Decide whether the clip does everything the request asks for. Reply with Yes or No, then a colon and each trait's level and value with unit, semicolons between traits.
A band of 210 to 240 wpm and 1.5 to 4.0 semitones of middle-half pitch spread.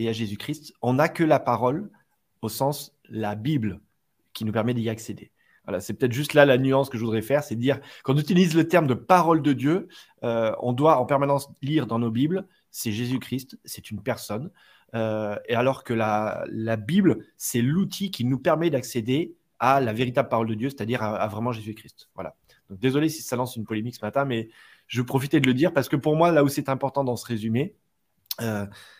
No: average, 215 wpm; average, 4.4 semitones